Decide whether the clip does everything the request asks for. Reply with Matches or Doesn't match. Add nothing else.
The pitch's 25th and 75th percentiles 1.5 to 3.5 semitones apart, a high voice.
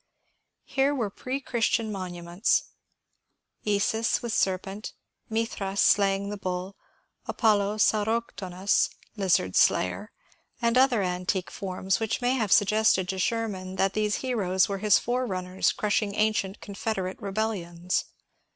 Matches